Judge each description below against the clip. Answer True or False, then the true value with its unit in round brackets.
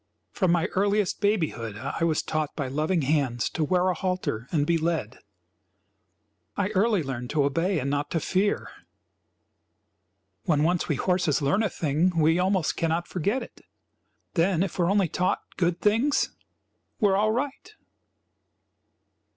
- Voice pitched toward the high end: False (170 Hz)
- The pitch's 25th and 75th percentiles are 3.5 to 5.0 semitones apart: True (4.1 semitones)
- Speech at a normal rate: True (155 wpm)